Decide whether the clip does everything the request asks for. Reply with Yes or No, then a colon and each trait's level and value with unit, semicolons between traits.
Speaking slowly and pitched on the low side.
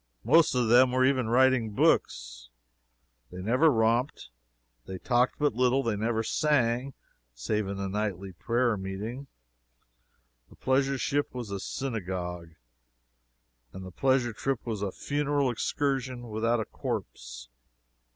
Yes: slow, 130 wpm; low, 120 Hz